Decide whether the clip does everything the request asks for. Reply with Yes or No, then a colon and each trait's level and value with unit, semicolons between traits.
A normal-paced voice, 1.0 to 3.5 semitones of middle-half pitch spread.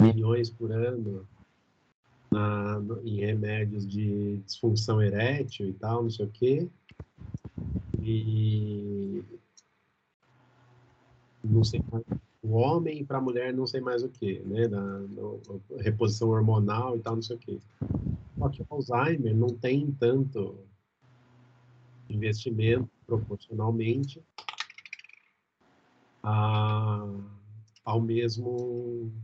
No: slow, 110 wpm; narrow, 2.6 semitones